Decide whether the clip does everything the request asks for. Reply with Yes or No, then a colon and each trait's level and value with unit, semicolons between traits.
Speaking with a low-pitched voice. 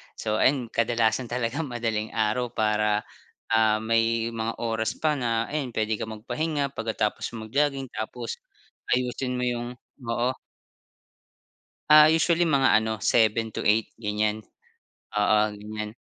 Yes: low, 115 Hz